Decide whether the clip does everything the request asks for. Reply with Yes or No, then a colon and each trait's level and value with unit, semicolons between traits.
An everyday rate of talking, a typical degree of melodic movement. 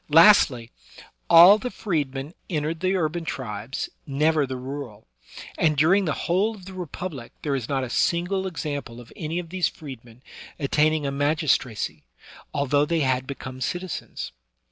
Yes: average, 155 wpm; average, 4.6 semitones